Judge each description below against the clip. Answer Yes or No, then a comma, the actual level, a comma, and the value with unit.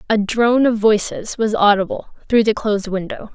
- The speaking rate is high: No, average, 180 wpm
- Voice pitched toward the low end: No, high, 215 Hz